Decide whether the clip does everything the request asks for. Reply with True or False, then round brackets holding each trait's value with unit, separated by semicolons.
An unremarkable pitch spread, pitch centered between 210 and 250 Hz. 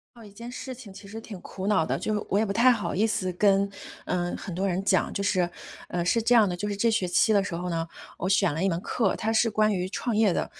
False (3.2 semitones; 200 Hz)